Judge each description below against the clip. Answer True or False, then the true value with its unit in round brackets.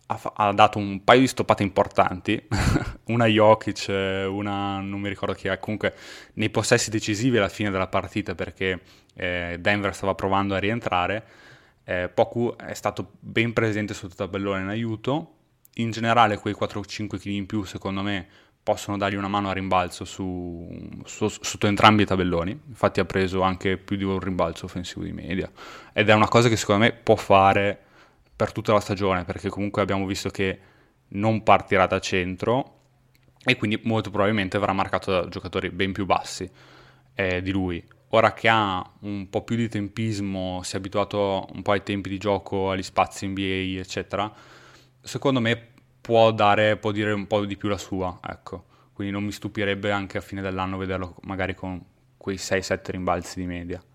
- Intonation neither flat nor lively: False (2.2 semitones)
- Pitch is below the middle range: True (100 Hz)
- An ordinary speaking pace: False (180 wpm)